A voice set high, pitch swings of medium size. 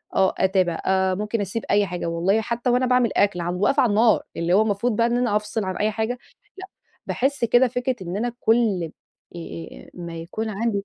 Yes: high, 210 Hz; average, 4.1 semitones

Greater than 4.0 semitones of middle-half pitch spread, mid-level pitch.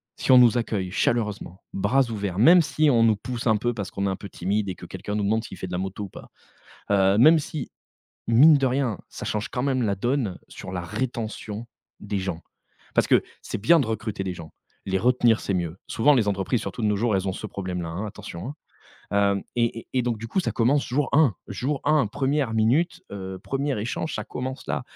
No: average, 4.7 semitones; low, 110 Hz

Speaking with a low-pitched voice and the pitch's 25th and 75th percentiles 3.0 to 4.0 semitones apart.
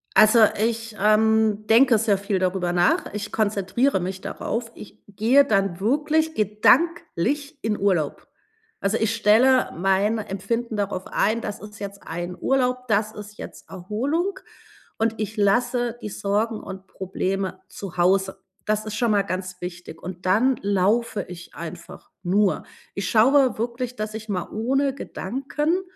No: high, 210 Hz; average, 3.5 semitones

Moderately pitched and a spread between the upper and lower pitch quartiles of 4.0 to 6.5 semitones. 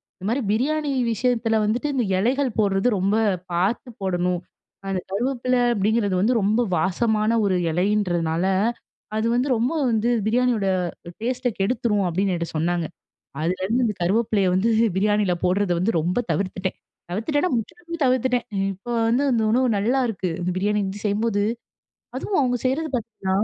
No: high, 215 Hz; average, 4.4 semitones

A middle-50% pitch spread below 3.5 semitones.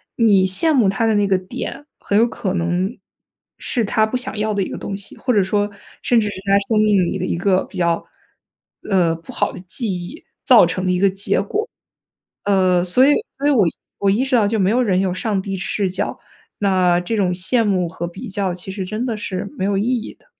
Yes: average, 3.0 semitones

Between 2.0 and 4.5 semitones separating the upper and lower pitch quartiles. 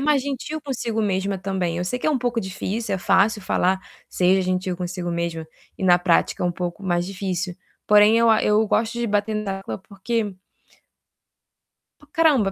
Yes: average, 3.6 semitones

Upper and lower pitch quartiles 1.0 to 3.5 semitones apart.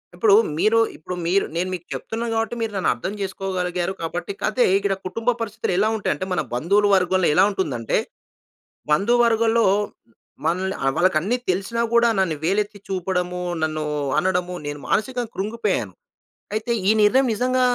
No: average, 3.9 semitones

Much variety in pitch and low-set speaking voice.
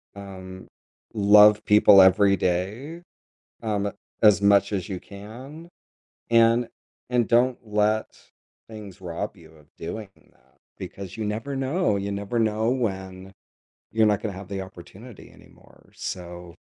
No: average, 2.9 semitones; low, 100 Hz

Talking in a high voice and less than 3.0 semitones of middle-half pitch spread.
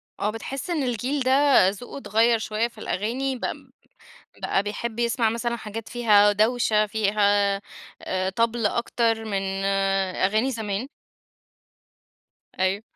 Yes: high, 225 Hz; narrow, 2.4 semitones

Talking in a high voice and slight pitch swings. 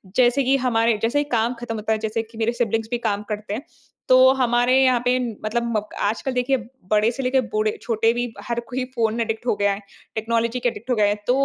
Yes: high, 230 Hz; narrow, 2.1 semitones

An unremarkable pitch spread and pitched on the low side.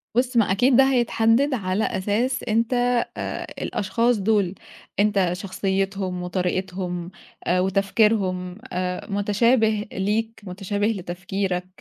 No: average, 3.3 semitones; high, 200 Hz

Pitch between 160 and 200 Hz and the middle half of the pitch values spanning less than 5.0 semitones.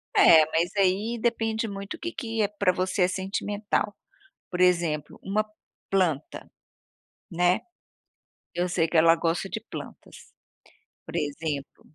Yes: medium, 185 Hz; average, 3.8 semitones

